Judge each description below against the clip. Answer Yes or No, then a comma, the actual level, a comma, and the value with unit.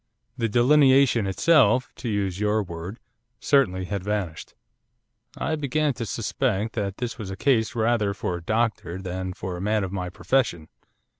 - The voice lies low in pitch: Yes, low, 105 Hz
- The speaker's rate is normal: Yes, average, 160 wpm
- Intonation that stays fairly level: No, average, 4.6 semitones